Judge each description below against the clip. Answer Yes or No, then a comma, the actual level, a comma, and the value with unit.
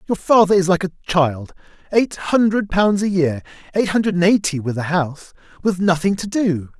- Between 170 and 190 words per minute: Yes, average, 175 wpm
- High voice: No, medium, 180 Hz